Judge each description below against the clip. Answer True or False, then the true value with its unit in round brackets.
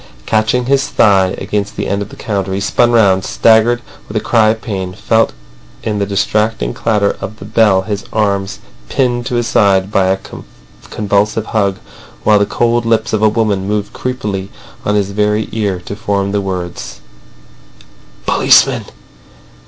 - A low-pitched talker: True (105 Hz)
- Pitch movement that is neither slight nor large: False (2.1 semitones)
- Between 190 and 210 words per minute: False (165 wpm)